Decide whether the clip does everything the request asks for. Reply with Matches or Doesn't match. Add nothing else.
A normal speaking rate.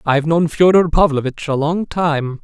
Matches